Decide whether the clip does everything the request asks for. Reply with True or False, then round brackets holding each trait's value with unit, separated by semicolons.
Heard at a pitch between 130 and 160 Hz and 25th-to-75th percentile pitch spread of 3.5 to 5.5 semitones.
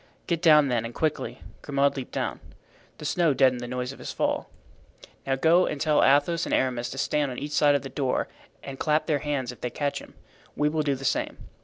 False (140 Hz; 2.5 semitones)